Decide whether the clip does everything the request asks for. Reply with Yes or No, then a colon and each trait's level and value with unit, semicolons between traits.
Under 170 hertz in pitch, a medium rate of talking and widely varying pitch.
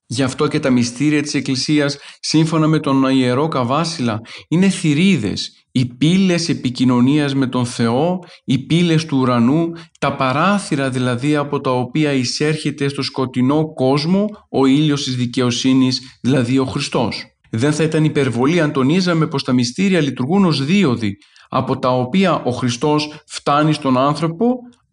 No: medium, 140 Hz; average, 145 wpm; average, 3.5 semitones